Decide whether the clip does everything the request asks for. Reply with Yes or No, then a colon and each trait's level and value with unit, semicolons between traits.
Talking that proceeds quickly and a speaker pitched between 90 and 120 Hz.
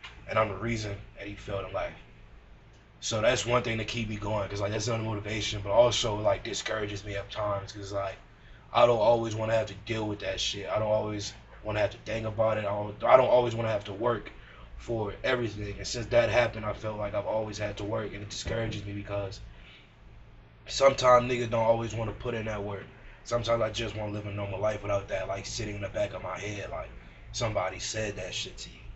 Yes: fast, 240 wpm; low, 105 Hz